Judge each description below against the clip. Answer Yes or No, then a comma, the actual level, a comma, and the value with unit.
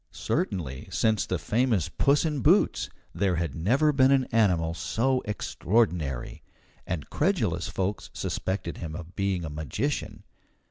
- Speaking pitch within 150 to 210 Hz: No, very low, 95 Hz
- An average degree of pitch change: No, wide, 6.1 semitones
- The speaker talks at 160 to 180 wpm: No, slow, 135 wpm